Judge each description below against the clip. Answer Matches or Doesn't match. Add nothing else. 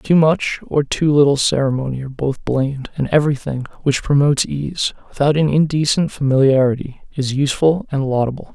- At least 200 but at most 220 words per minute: Doesn't match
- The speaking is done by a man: Matches